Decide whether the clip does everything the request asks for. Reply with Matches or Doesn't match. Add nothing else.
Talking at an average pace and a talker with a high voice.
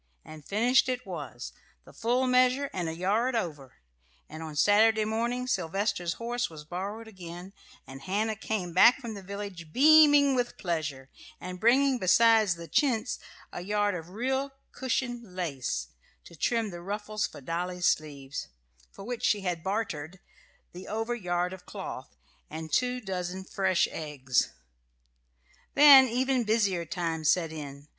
Matches